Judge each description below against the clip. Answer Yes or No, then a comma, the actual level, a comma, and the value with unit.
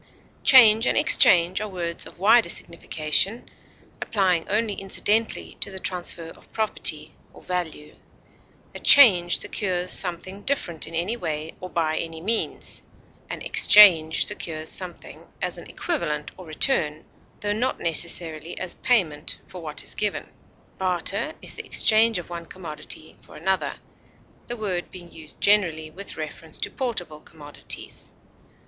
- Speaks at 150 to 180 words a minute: No, average, 140 wpm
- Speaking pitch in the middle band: Yes, medium, 180 Hz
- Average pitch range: Yes, average, 4.3 semitones